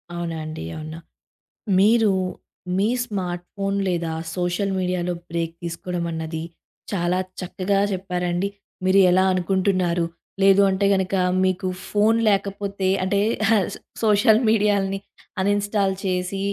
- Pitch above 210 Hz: No, high, 190 Hz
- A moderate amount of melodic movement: No, narrow, 2.1 semitones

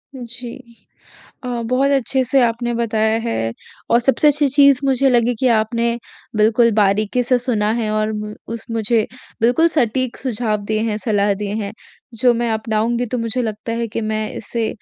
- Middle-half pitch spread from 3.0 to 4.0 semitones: No, narrow, 2.5 semitones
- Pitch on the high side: Yes, high, 230 Hz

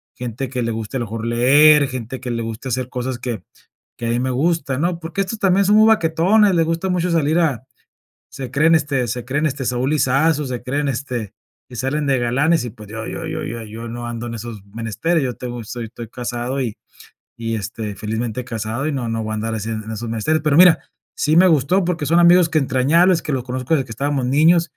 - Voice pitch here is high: No, low, 130 Hz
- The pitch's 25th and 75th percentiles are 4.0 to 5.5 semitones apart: Yes, average, 5.1 semitones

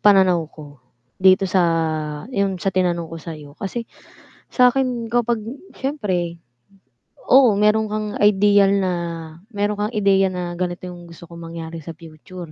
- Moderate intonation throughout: Yes, average, 3.8 semitones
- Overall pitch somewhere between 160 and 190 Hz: Yes, medium, 185 Hz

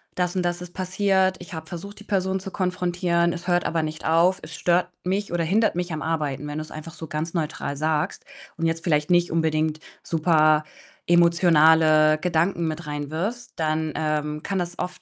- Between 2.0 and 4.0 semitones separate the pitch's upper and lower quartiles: Yes, narrow, 2.5 semitones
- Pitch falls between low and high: Yes, medium, 165 Hz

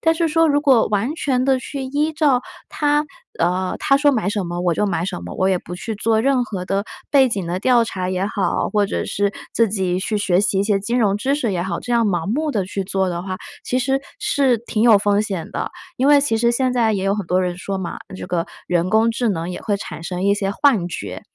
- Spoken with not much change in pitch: No, average, 5.2 semitones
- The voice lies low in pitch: No, high, 210 Hz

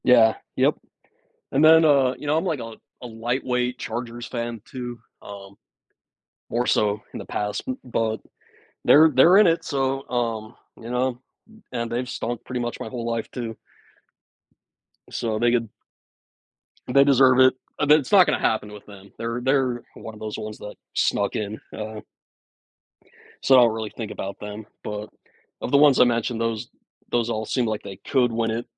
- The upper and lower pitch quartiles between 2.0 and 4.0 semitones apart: Yes, average, 2.8 semitones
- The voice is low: Yes, low, 120 Hz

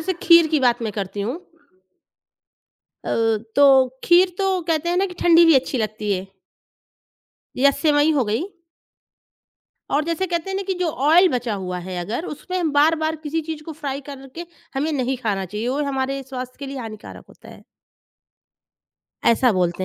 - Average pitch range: No, wide, 6.1 semitones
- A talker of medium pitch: No, very high, 280 Hz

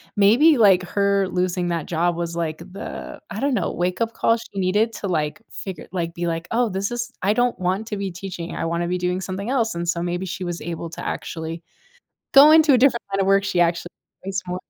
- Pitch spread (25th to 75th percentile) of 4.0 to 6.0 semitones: No, average, 3.4 semitones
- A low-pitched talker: No, medium, 185 Hz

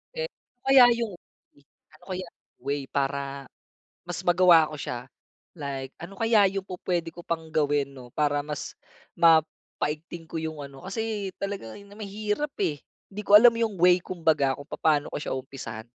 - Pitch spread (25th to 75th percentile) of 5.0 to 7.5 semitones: Yes, wide, 5.6 semitones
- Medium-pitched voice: Yes, medium, 165 Hz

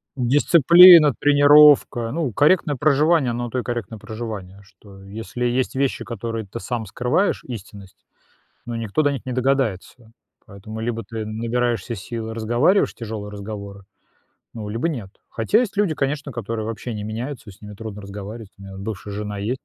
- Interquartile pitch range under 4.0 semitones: No, average, 4.4 semitones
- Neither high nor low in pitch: No, low, 115 Hz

